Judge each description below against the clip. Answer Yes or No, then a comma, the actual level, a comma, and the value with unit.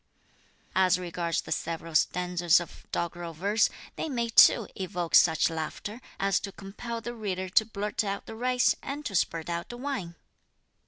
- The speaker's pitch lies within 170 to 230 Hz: Yes, high, 190 Hz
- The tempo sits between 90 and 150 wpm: No, average, 165 wpm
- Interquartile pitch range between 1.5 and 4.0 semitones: No, average, 4.8 semitones